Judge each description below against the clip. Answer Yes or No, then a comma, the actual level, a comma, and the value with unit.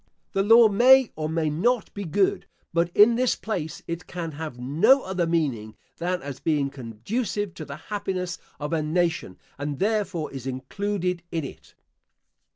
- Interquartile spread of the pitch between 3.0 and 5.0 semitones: No, wide, 5.5 semitones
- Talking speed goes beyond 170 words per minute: No, average, 165 wpm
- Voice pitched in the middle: Yes, medium, 170 Hz